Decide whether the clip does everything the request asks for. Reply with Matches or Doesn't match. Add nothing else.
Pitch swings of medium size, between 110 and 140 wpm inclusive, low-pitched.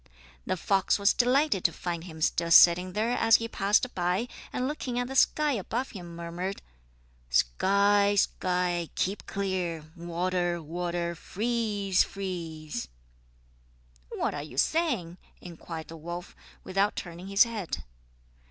Doesn't match